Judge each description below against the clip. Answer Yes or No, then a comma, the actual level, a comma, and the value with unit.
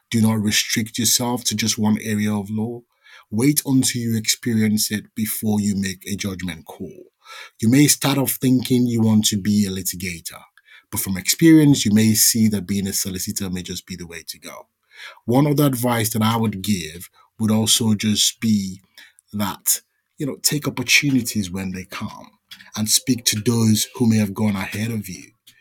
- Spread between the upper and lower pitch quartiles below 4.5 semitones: Yes, average, 2.7 semitones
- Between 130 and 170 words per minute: No, average, 185 wpm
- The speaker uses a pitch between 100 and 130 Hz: Yes, low, 110 Hz